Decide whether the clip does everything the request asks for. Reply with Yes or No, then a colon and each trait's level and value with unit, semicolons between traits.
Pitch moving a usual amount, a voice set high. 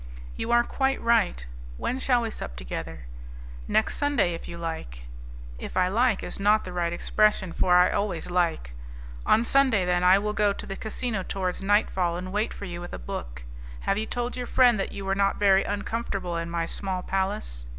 Yes: average, 3.9 semitones; high, 195 Hz